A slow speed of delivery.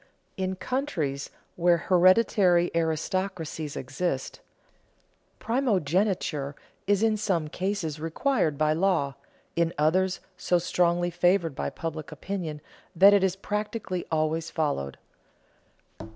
Yes: slow, 105 wpm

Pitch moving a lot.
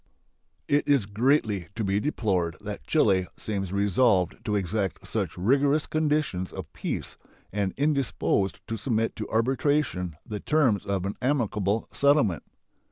Yes: wide, 6.1 semitones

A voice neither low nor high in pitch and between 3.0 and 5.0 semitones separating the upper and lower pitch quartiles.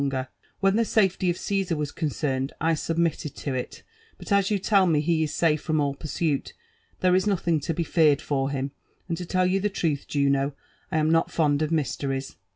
Yes: medium, 160 Hz; average, 4.2 semitones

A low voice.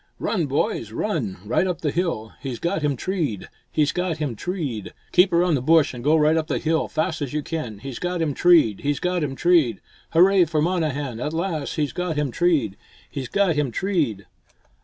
No: medium, 155 Hz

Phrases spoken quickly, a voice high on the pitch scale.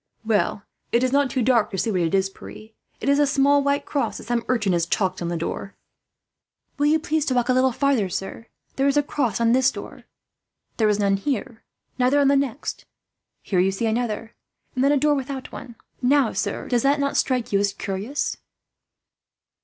Yes: fast, 210 wpm; high, 245 Hz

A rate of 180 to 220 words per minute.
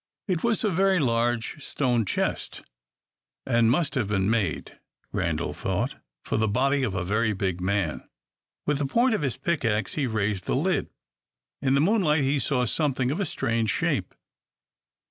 No: average, 165 wpm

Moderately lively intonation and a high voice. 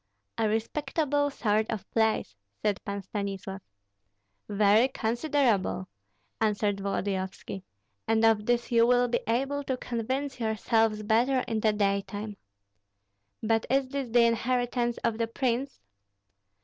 Yes: average, 3.0 semitones; high, 225 Hz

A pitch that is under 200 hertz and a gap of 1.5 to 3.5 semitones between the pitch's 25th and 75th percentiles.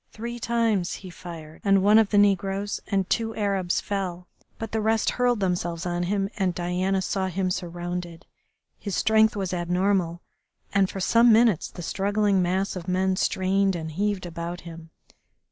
Yes: high, 190 Hz; narrow, 2.6 semitones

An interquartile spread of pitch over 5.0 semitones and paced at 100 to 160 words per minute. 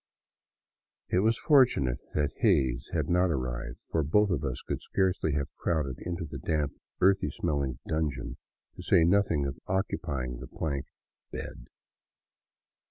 Yes: wide, 5.4 semitones; average, 145 wpm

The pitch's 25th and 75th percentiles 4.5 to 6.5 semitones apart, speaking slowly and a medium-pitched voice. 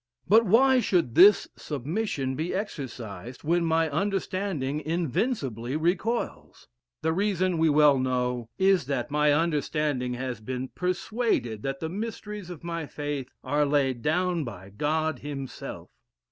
Yes: wide, 5.6 semitones; slow, 130 wpm; medium, 150 Hz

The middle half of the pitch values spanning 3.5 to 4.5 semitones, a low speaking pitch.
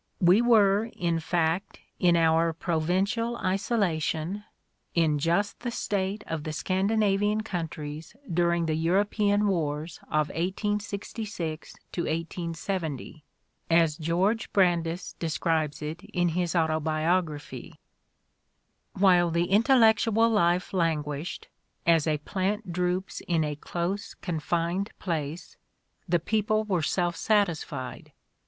No: average, 3.8 semitones; medium, 175 Hz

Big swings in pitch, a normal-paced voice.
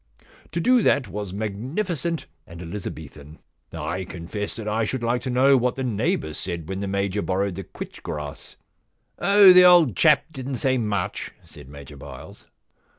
Yes: wide, 6.6 semitones; average, 170 wpm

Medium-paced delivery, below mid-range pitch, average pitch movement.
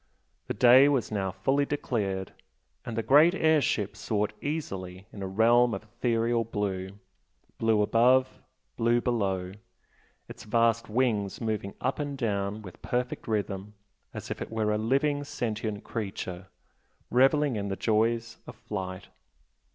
Yes: average, 145 wpm; low, 115 Hz; average, 3.5 semitones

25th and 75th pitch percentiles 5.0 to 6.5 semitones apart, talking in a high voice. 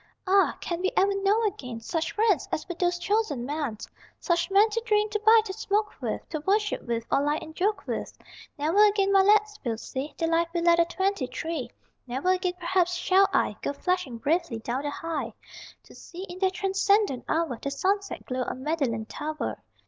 Yes: wide, 5.6 semitones; very high, 350 Hz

